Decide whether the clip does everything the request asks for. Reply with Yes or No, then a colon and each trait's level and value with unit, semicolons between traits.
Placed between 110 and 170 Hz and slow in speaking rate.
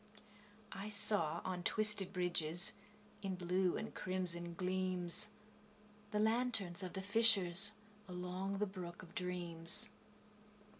No: medium, 185 Hz; slow, 110 wpm